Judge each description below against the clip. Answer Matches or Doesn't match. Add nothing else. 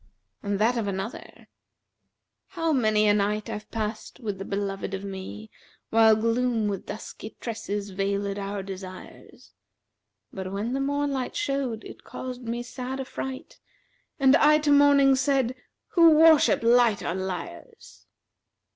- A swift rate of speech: Doesn't match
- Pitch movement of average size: Matches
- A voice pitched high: Matches